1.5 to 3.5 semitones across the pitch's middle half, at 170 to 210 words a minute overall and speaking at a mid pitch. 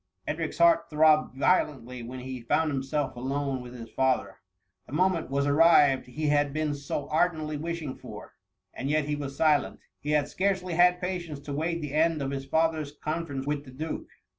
Yes: average, 2.9 semitones; average, 195 wpm; medium, 150 Hz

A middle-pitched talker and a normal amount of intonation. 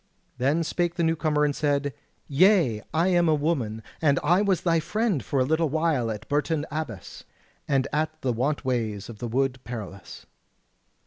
Yes: medium, 145 Hz; average, 4.6 semitones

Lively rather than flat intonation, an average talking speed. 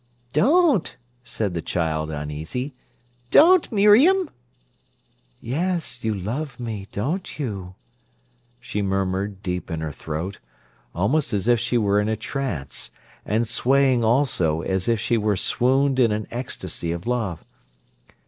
No: wide, 6.2 semitones; slow, 130 wpm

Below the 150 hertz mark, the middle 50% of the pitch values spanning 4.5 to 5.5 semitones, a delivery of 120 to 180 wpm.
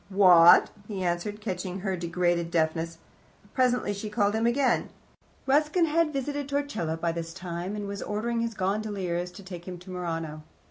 No: high, 190 Hz; average, 5.0 semitones; average, 160 wpm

